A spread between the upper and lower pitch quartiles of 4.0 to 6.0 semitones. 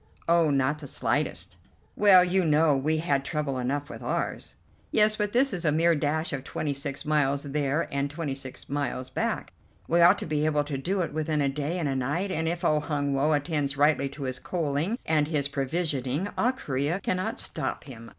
No: average, 3.2 semitones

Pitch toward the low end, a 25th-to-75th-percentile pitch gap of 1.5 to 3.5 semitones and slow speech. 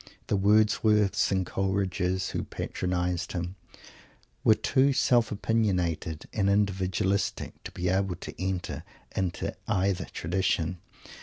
Yes: very low, 95 Hz; narrow, 2.5 semitones; slow, 110 wpm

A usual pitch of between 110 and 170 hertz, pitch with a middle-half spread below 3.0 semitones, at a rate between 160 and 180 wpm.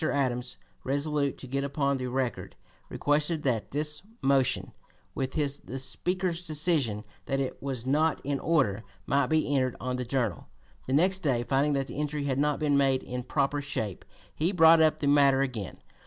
Yes: medium, 140 Hz; narrow, 2.5 semitones; average, 175 wpm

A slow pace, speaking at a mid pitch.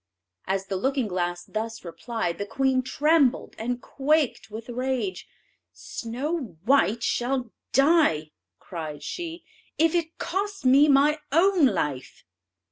No: slow, 125 wpm; very high, 255 Hz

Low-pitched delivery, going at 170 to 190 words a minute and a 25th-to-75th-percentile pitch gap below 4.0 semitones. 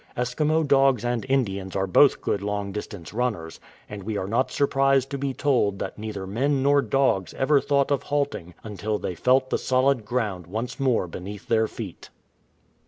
No: low, 120 Hz; average, 180 wpm; average, 5.1 semitones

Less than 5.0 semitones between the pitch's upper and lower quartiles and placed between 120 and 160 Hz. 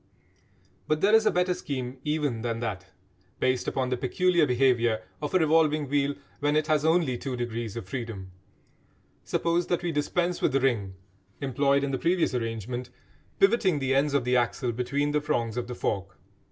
Yes: average, 4.3 semitones; low, 135 Hz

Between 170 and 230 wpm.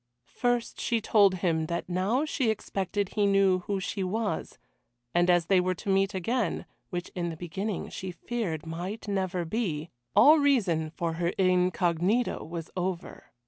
No: average, 160 wpm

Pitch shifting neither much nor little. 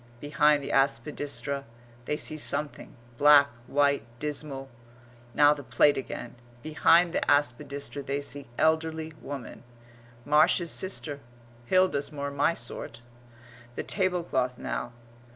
No: narrow, 1.8 semitones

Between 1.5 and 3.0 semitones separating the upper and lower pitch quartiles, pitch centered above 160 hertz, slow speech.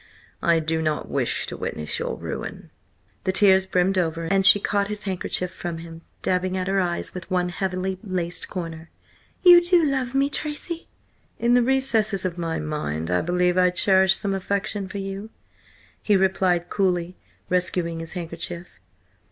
No: average, 2.7 semitones; medium, 185 Hz; average, 165 wpm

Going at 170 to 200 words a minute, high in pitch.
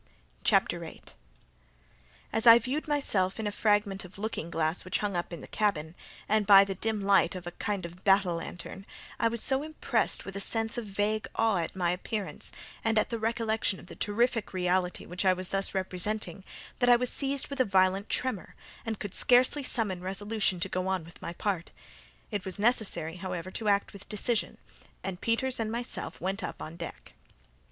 Yes: average, 195 wpm; high, 200 Hz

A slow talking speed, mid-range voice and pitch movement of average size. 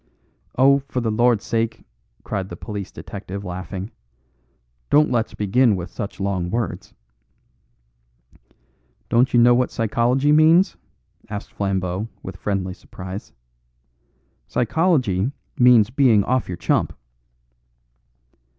No: slow, 110 wpm; low, 110 Hz; average, 4.4 semitones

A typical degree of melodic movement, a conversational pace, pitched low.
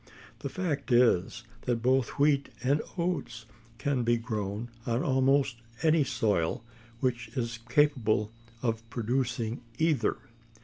No: average, 3.4 semitones; slow, 120 wpm; low, 125 Hz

